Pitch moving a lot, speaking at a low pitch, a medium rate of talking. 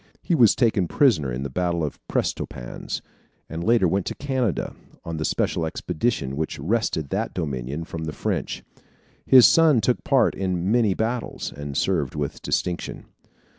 Yes: wide, 7.2 semitones; very low, 90 Hz; average, 160 wpm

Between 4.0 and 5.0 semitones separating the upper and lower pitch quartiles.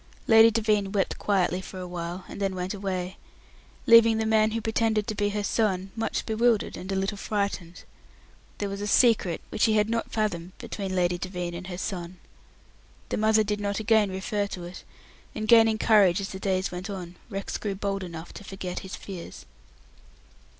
No: average, 2.7 semitones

